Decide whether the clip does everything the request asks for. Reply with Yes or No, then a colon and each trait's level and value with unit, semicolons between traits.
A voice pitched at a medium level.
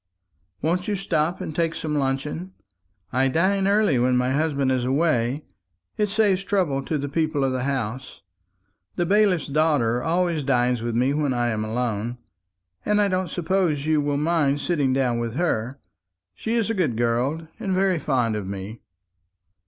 Yes: medium, 145 Hz